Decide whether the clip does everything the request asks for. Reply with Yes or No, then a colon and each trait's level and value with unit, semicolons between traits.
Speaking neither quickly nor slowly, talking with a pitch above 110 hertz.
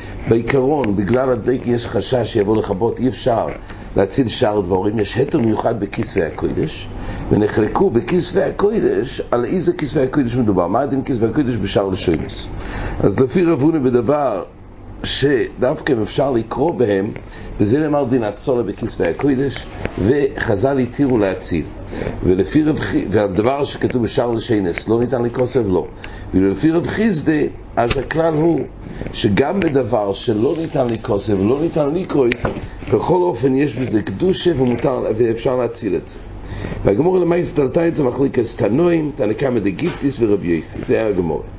Yes: average, 145 wpm; low, 125 Hz